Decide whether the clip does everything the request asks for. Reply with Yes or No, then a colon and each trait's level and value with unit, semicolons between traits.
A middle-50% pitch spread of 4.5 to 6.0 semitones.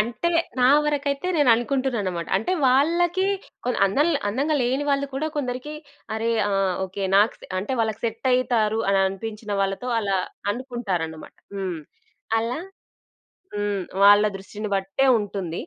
Yes: average, 5.2 semitones